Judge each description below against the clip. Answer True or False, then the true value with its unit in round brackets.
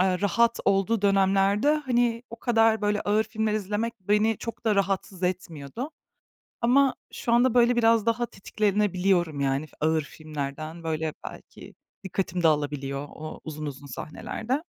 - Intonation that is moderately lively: False (6.2 semitones)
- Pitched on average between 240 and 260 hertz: False (200 Hz)